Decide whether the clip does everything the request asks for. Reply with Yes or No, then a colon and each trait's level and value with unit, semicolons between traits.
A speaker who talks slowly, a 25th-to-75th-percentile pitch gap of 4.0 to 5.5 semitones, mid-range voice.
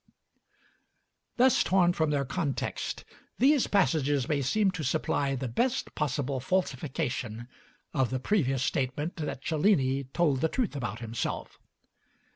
Yes: slow, 125 wpm; average, 5.1 semitones; medium, 145 Hz